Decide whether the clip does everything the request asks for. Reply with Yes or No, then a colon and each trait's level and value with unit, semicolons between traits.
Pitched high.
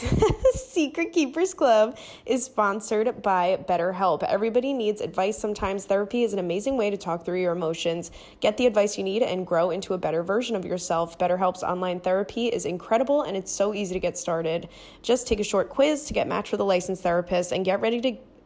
Yes: high, 195 Hz